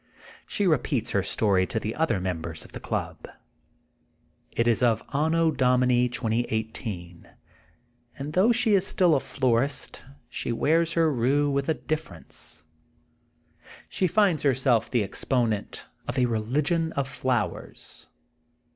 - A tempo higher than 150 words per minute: No, slow, 135 wpm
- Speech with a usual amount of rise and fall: No, wide, 5.8 semitones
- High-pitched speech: No, low, 130 Hz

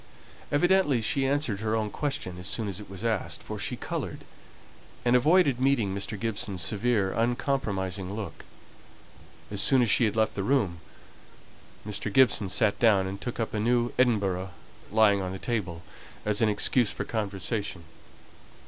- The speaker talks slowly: No, average, 160 wpm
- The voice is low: Yes, low, 110 Hz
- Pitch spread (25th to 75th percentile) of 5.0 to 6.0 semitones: No, average, 3.8 semitones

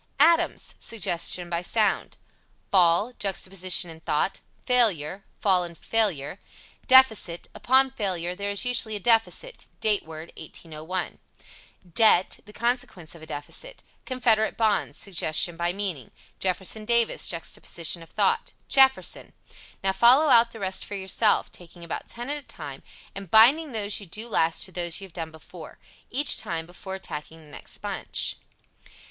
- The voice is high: Yes, high, 195 Hz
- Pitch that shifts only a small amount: No, average, 5.2 semitones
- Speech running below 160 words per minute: Yes, average, 150 wpm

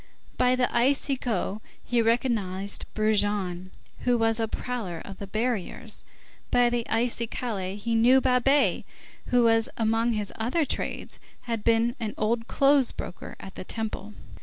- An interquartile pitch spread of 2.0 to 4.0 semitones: Yes, average, 2.8 semitones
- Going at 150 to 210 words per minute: No, slow, 135 wpm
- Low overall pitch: No, high, 230 Hz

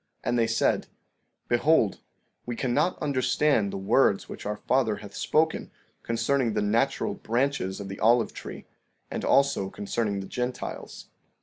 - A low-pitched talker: Yes, low, 115 Hz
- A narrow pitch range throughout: No, average, 4.6 semitones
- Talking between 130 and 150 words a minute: Yes, average, 145 wpm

